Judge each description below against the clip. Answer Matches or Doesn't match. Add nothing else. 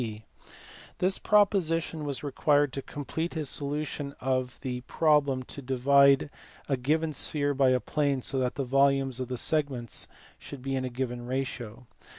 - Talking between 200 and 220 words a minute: Doesn't match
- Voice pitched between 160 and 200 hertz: Doesn't match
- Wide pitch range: Doesn't match